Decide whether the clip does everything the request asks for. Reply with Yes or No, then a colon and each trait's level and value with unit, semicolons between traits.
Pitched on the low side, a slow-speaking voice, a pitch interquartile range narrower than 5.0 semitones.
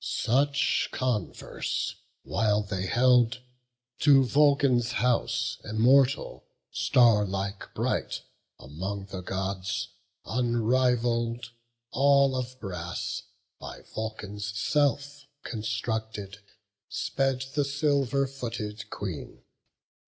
Yes: low, 115 Hz; slow, 80 wpm; average, 4.4 semitones